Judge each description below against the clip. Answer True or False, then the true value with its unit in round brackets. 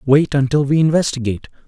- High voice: False (140 Hz)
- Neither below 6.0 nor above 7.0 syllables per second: True (6.5 syllables/s)